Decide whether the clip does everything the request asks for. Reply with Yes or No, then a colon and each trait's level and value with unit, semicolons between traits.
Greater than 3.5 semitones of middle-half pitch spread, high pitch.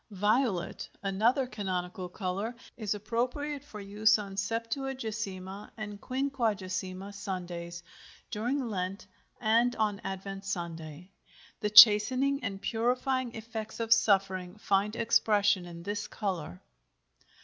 No: average, 3.2 semitones; high, 210 Hz